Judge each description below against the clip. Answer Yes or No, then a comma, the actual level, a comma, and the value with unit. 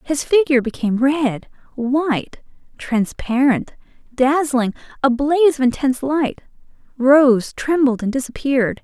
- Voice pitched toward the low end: No, very high, 265 Hz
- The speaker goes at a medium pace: No, slow, 95 wpm